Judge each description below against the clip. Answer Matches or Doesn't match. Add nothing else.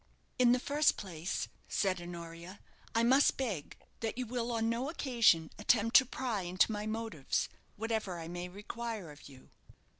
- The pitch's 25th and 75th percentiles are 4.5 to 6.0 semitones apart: Matches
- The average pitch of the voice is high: Matches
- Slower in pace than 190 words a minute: Matches